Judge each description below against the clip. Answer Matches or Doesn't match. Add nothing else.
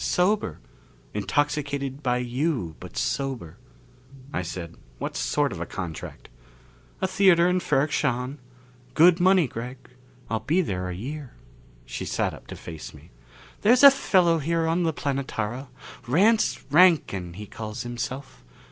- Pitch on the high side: Doesn't match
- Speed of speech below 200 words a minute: Matches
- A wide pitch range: Matches